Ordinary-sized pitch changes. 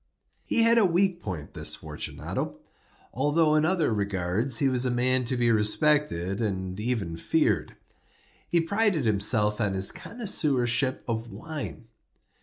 No: wide, 6.8 semitones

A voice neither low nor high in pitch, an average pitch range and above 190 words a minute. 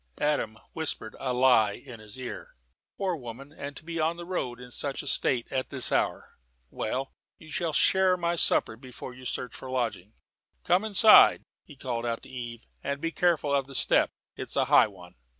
No: low, 130 Hz; average, 4.9 semitones; average, 200 wpm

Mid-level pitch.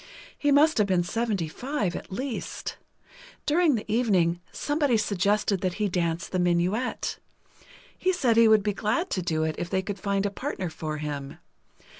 No: high, 200 Hz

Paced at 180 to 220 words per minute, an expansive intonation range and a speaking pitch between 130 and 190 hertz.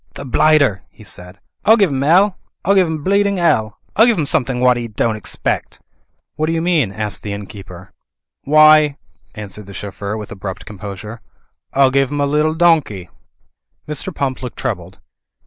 Yes: average, 200 wpm; wide, 7.2 semitones; low, 135 Hz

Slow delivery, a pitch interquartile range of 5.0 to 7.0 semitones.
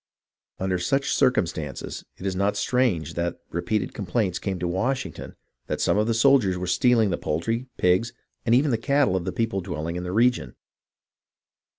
No: average, 175 wpm; wide, 5.4 semitones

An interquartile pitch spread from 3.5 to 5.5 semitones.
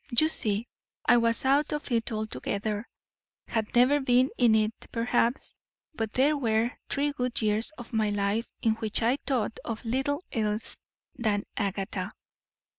No: average, 3.1 semitones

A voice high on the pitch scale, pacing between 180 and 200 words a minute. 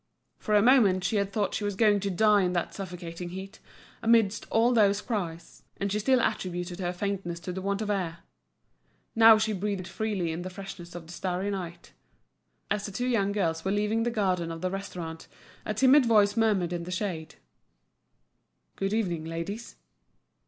Yes: high, 195 Hz; average, 185 wpm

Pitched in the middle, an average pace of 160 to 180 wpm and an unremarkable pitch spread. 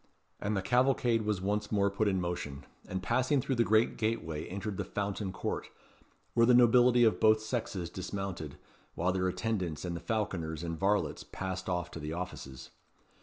No: low, 100 Hz; average, 175 wpm; average, 4.1 semitones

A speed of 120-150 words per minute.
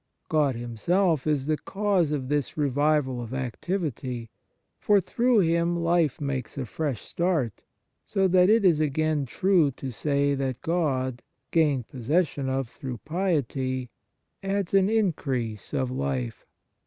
Yes: average, 140 wpm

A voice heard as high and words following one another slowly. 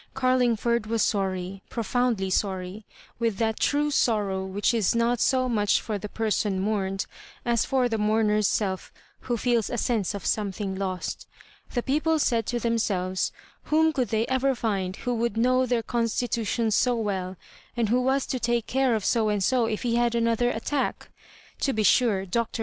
No: high, 225 Hz; average, 180 wpm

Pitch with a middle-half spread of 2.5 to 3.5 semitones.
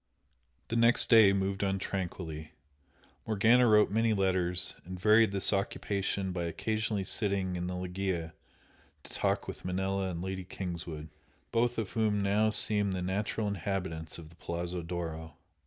Yes: average, 2.9 semitones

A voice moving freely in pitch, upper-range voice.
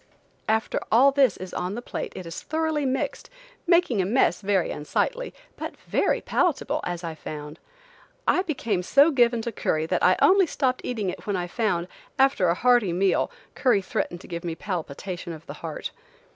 Yes: wide, 7.1 semitones; high, 205 Hz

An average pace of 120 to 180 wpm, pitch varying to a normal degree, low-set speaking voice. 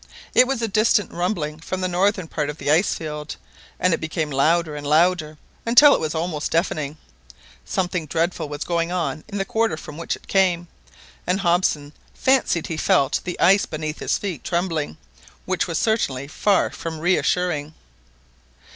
No: average, 170 wpm; average, 3.4 semitones; medium, 170 Hz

